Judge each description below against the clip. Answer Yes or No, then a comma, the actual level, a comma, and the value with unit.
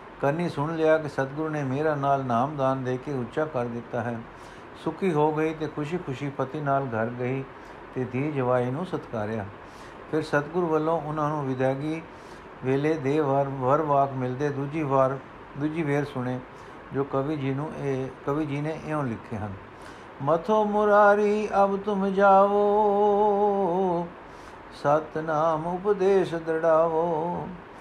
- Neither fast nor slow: Yes, average, 140 wpm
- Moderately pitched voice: Yes, medium, 150 Hz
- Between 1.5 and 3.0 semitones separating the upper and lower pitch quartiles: No, average, 3.7 semitones